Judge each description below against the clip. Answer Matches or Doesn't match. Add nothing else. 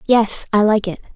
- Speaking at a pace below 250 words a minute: Matches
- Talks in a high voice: Matches